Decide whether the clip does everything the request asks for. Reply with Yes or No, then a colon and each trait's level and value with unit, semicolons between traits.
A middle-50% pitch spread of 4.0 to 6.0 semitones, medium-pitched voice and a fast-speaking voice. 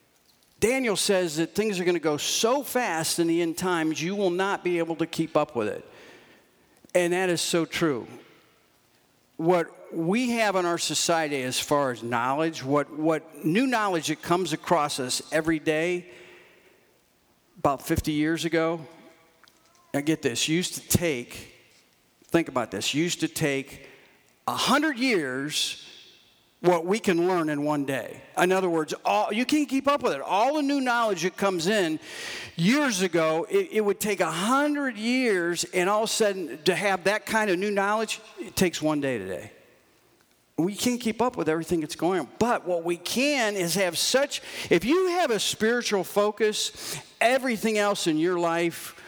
No: average, 5.1 semitones; medium, 175 Hz; average, 175 wpm